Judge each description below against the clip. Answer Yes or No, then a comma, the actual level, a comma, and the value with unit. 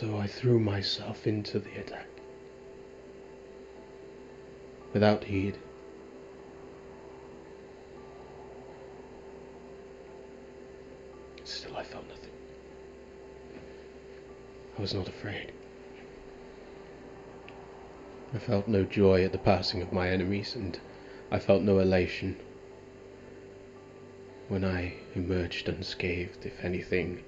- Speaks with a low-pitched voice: Yes, very low, 95 Hz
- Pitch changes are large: Yes, wide, 7.6 semitones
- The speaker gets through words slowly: Yes, slow, 85 wpm